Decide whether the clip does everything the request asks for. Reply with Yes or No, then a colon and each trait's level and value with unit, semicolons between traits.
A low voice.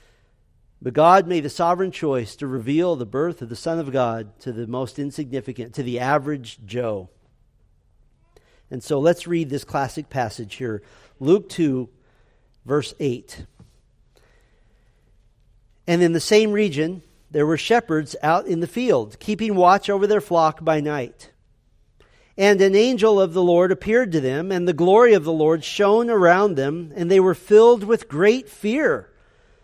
No: medium, 155 Hz